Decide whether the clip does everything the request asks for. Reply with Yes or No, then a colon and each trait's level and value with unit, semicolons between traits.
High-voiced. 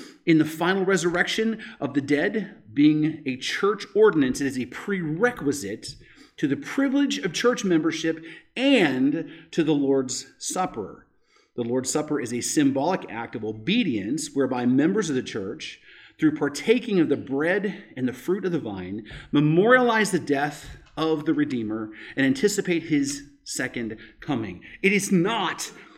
No: medium, 160 Hz